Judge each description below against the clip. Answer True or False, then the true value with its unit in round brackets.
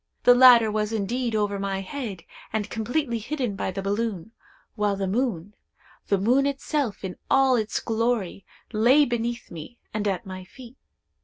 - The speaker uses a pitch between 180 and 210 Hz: False (220 Hz)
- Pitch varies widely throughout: False (3.7 semitones)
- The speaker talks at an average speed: True (150 wpm)